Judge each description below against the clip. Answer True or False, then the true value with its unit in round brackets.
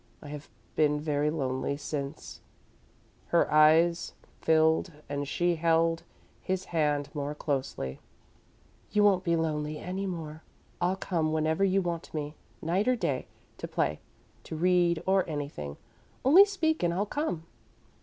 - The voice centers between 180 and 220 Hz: False (160 Hz)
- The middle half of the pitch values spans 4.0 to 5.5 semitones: False (3.4 semitones)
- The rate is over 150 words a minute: False (145 wpm)